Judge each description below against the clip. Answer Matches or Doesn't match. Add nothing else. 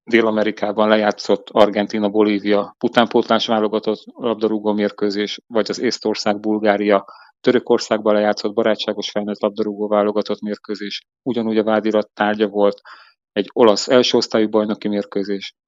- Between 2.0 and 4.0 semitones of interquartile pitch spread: Doesn't match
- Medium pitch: Doesn't match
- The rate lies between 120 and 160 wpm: Doesn't match